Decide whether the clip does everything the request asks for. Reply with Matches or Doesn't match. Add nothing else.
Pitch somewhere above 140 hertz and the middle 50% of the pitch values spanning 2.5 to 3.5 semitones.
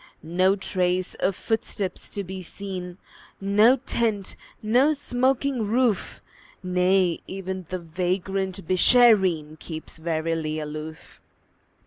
Matches